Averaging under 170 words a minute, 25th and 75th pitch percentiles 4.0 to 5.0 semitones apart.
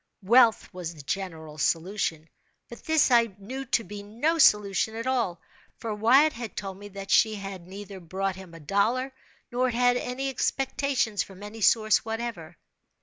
Yes: average, 155 wpm; average, 4.4 semitones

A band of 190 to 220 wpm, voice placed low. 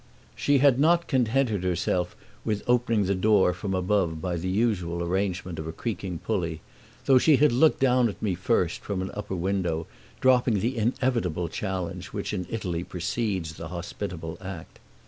No: average, 165 wpm; very low, 95 Hz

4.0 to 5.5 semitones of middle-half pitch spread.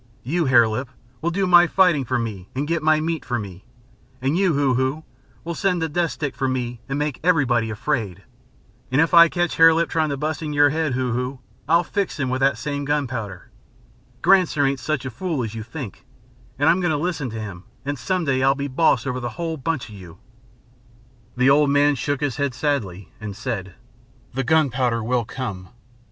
Yes: average, 4.6 semitones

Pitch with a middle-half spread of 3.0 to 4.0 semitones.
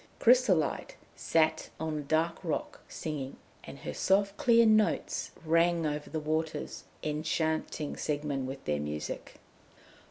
No: narrow, 2.5 semitones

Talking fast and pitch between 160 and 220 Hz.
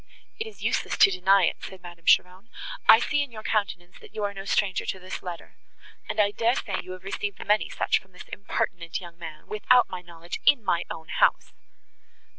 Yes: fast, 210 wpm; high, 190 Hz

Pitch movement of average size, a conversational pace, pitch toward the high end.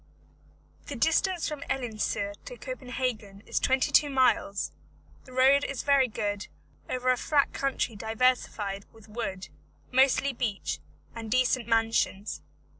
No: average, 3.9 semitones; slow, 125 wpm; very high, 250 Hz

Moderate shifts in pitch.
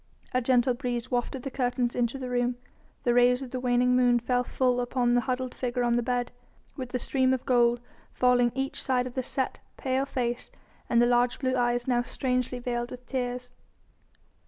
No: narrow, 0.8 semitones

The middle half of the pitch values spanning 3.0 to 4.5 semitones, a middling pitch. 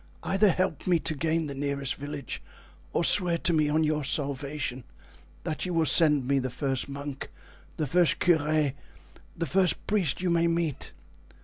Yes: average, 3.3 semitones; medium, 155 Hz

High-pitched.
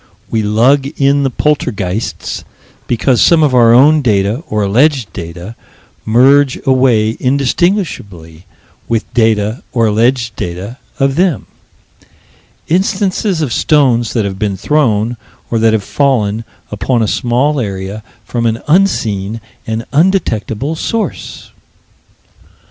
No: low, 120 Hz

